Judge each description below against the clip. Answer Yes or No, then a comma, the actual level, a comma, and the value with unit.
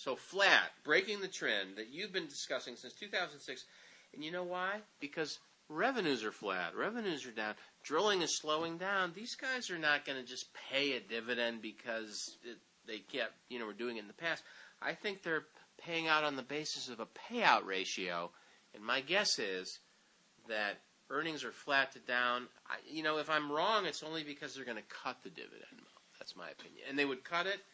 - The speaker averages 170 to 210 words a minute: Yes, average, 200 wpm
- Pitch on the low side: No, medium, 145 Hz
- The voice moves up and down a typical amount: No, wide, 5.8 semitones